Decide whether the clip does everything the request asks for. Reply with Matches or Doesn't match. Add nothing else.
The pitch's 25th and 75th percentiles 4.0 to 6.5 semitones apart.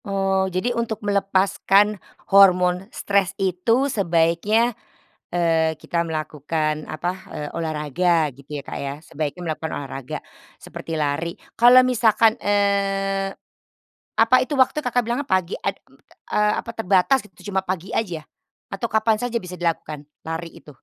Matches